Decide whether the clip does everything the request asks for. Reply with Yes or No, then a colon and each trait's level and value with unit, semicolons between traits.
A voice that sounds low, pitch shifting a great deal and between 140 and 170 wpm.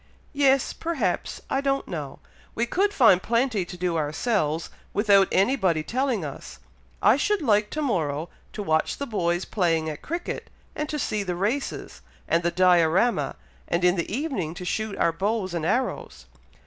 No: high, 200 Hz; wide, 7.0 semitones; average, 165 wpm